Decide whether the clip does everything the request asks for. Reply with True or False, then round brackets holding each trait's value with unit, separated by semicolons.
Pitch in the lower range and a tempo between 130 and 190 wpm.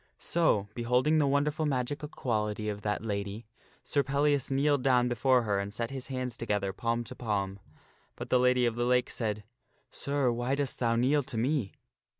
True (125 Hz; 185 wpm)